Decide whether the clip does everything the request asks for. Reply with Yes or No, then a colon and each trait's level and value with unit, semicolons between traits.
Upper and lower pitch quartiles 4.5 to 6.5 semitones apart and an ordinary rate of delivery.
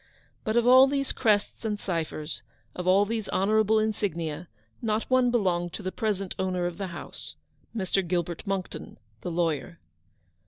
No: average, 3.8 semitones; average, 160 wpm